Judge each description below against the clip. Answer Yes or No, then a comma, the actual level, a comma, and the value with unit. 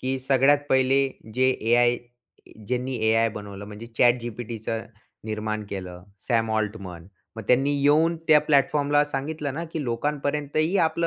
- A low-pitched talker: Yes, low, 130 Hz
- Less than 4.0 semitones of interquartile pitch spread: No, average, 4.6 semitones